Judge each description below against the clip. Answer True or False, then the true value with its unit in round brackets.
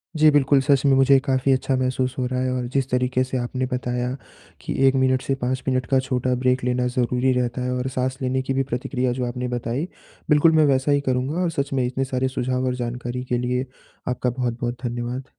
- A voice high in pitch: False (130 Hz)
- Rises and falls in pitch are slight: True (1.0 semitones)